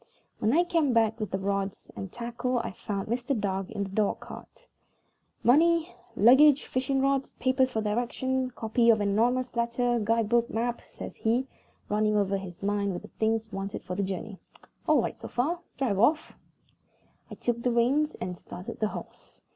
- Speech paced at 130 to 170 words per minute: No, average, 180 wpm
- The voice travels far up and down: No, average, 4.0 semitones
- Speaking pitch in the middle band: No, high, 230 Hz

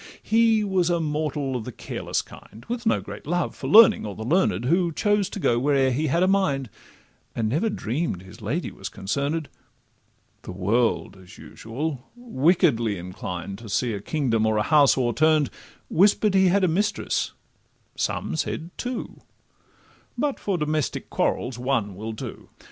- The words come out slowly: No, average, 165 wpm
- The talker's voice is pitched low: No, medium, 145 Hz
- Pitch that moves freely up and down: Yes, wide, 8.3 semitones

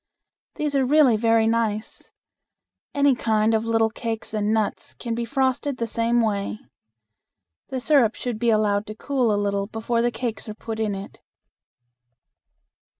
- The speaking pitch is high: Yes, high, 225 Hz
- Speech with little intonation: Yes, narrow, 2.1 semitones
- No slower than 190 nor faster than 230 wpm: No, average, 155 wpm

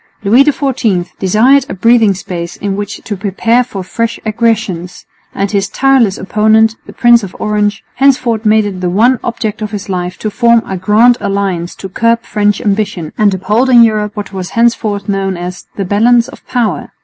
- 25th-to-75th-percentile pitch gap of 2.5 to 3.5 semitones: Yes, average, 3.1 semitones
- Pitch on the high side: Yes, high, 210 Hz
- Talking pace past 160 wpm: Yes, average, 185 wpm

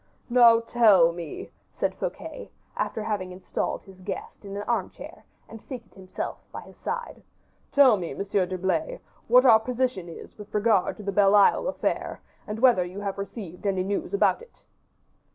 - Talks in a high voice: Yes, high, 205 Hz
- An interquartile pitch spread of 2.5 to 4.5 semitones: Yes, average, 3.7 semitones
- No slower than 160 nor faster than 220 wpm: Yes, average, 170 wpm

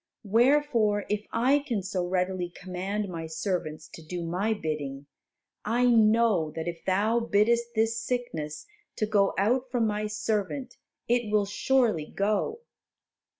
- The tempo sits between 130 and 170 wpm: Yes, average, 140 wpm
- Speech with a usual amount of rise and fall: Yes, average, 4.5 semitones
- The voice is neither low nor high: No, high, 210 Hz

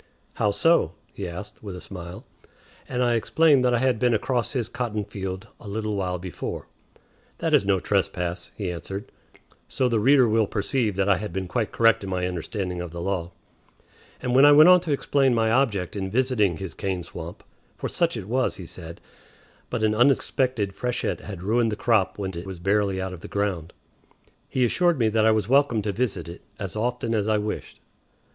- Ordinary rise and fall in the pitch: Yes, average, 4.5 semitones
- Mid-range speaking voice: No, low, 105 Hz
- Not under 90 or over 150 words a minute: No, fast, 205 wpm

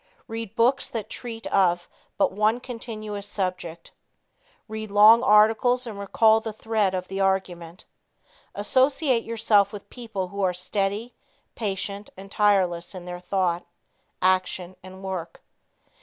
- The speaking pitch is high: Yes, high, 205 Hz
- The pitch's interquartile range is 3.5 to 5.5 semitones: No, average, 3.0 semitones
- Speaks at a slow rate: Yes, slow, 130 wpm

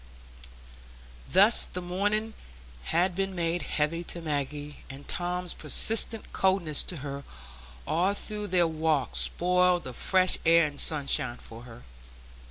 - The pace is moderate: No, slow, 130 wpm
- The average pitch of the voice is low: No, medium, 170 Hz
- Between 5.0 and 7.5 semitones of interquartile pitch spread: No, average, 3.9 semitones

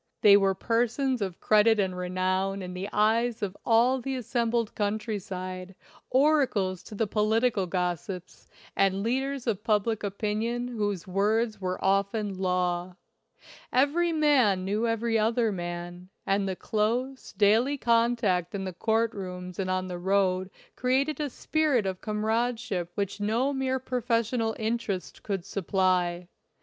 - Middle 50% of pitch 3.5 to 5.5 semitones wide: Yes, average, 4.0 semitones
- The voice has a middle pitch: No, high, 210 Hz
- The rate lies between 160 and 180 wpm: No, average, 140 wpm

